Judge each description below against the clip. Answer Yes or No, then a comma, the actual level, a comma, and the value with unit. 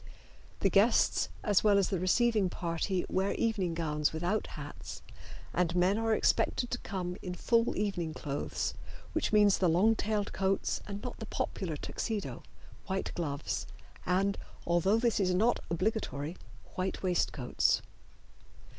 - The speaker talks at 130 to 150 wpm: Yes, average, 140 wpm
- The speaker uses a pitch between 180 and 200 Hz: Yes, high, 190 Hz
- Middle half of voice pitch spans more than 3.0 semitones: Yes, average, 3.5 semitones